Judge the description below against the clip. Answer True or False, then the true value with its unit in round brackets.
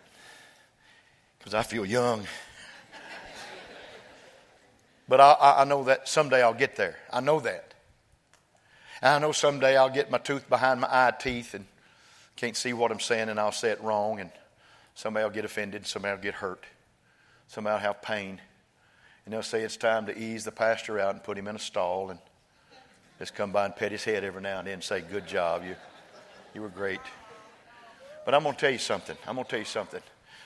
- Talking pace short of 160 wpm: False (200 wpm)